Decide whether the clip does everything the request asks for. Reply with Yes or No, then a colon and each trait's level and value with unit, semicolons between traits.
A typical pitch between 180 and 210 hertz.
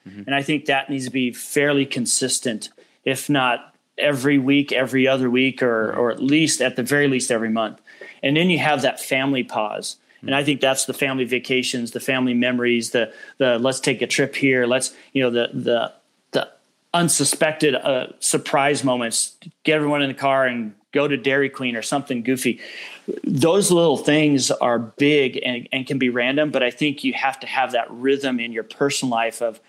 No: low, 135 Hz